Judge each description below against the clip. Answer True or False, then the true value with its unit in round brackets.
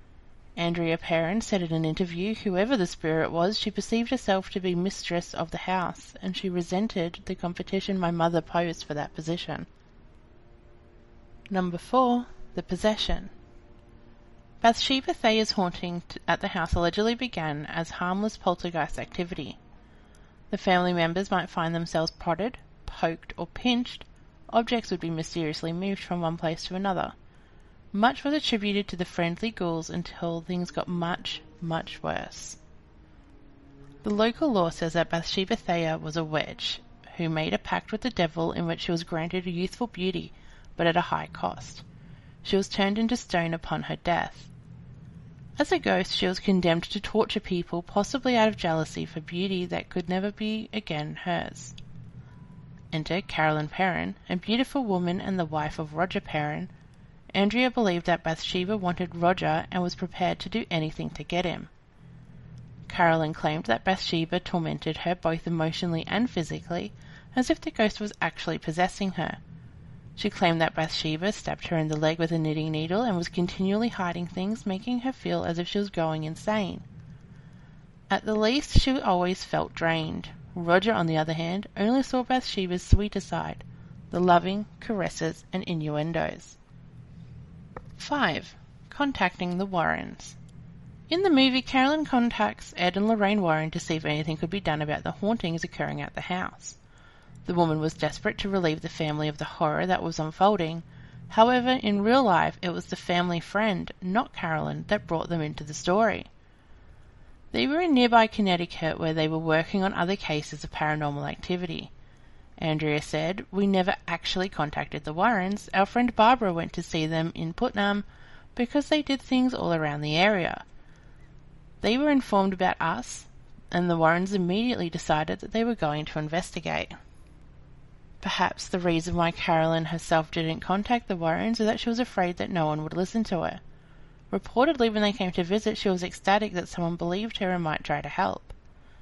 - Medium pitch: True (180 Hz)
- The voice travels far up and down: False (4.0 semitones)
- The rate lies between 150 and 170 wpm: True (165 wpm)